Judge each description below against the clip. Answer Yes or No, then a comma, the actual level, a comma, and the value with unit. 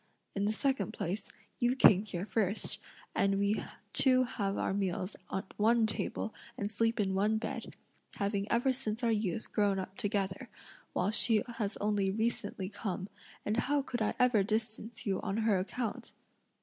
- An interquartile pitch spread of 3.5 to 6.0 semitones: No, narrow, 2.6 semitones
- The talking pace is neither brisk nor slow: Yes, average, 165 wpm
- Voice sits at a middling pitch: No, high, 210 Hz